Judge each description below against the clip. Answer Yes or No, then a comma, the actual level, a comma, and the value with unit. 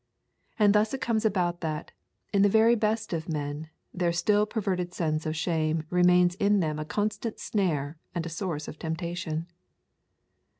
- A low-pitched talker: No, medium, 175 Hz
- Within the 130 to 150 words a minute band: No, average, 165 wpm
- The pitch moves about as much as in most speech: Yes, average, 4.5 semitones